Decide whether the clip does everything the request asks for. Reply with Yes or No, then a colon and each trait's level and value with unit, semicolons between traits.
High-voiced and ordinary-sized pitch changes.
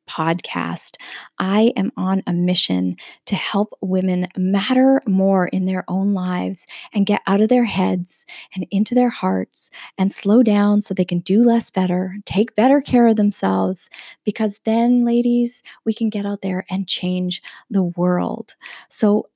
Yes: high, 195 Hz; average, 3.3 semitones